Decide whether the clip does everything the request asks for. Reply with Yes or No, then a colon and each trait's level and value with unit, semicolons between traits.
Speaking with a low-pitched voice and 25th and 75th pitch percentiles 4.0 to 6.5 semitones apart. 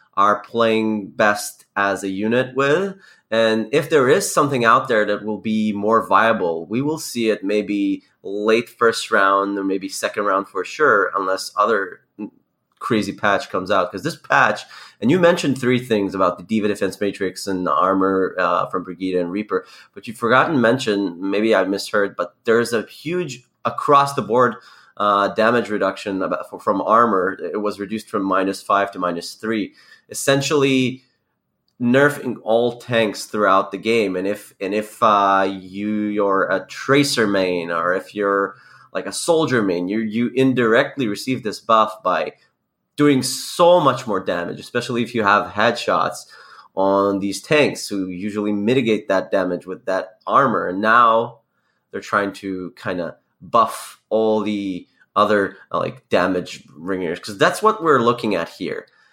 No: low, 105 Hz; average, 3.5 semitones